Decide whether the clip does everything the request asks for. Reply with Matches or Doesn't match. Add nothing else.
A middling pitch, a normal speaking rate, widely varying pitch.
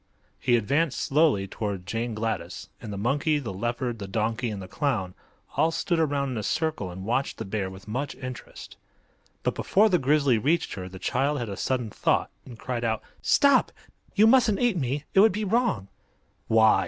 Doesn't match